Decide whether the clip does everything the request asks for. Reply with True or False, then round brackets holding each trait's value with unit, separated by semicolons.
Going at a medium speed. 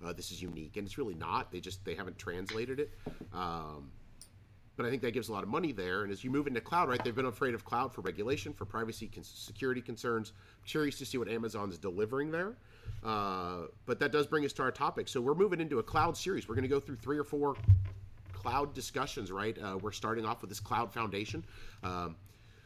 False (235 wpm)